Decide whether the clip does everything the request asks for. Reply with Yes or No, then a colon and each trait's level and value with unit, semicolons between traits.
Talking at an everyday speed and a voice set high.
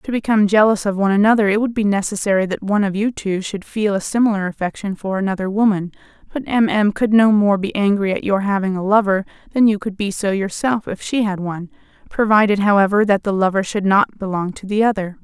No: fast, 225 wpm; high, 200 Hz